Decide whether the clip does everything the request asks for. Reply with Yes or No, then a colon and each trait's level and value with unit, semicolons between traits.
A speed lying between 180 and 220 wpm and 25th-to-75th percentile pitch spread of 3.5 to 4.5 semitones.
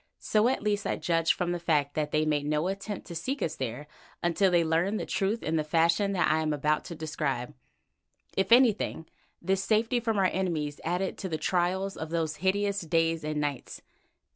Yes: average, 200 wpm; average, 4.0 semitones